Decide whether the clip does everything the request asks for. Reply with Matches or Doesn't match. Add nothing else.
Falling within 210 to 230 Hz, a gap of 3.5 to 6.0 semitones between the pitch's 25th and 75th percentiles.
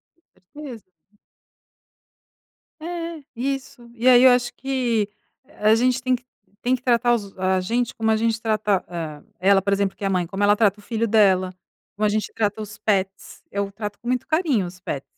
Matches